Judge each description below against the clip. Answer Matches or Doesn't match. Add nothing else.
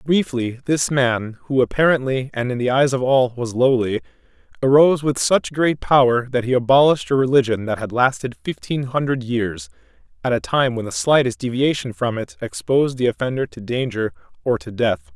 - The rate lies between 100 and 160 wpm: Doesn't match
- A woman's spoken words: Doesn't match